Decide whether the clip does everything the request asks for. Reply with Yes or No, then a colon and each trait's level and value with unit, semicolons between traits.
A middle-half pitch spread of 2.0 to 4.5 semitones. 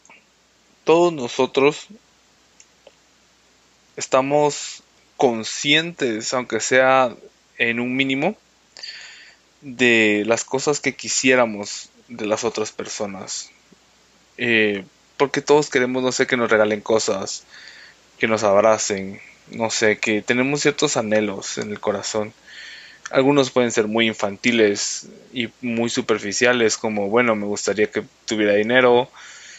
Yes: average, 3.5 semitones